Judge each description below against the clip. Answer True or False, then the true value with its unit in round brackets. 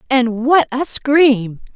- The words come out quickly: False (135 wpm)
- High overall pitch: True (255 Hz)